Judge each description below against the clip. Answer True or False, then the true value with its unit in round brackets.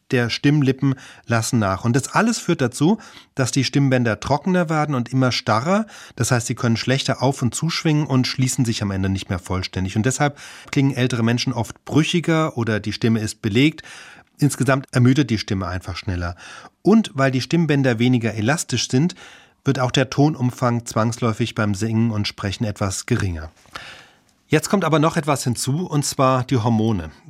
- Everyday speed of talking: True (175 wpm)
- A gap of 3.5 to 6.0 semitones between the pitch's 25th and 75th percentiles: True (4.2 semitones)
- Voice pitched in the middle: False (130 Hz)